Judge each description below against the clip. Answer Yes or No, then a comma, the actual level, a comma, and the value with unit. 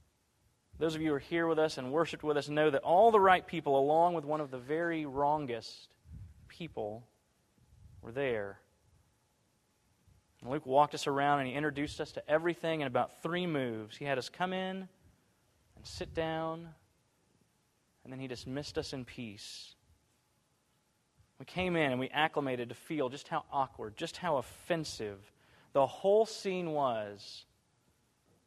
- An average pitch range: Yes, average, 4.9 semitones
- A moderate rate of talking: Yes, average, 160 wpm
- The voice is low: No, medium, 145 Hz